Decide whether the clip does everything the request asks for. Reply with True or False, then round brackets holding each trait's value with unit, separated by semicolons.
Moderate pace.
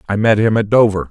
False (270 wpm)